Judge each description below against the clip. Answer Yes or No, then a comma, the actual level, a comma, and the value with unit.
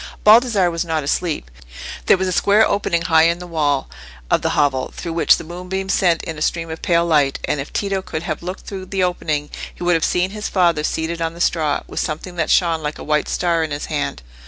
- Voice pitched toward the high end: No, medium, 170 Hz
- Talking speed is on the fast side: Yes, fast, 235 wpm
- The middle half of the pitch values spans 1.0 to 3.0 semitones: Yes, average, 2.7 semitones